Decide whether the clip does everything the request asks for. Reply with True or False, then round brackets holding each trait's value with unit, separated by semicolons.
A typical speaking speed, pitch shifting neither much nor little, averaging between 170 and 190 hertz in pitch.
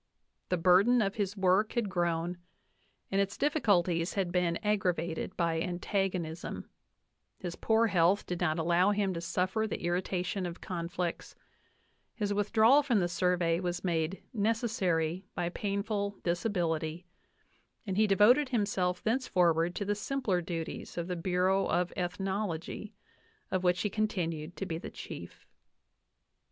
True (150 wpm; 3.0 semitones; 185 Hz)